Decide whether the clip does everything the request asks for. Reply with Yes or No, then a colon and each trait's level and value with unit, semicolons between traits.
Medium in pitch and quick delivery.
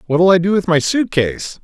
Yes: medium, 175 Hz; fast, 260 wpm